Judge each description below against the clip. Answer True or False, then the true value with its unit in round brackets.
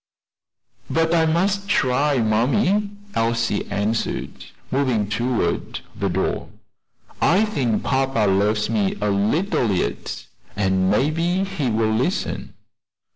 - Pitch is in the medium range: False (120 Hz)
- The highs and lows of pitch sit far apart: True (7.5 semitones)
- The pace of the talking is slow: True (110 wpm)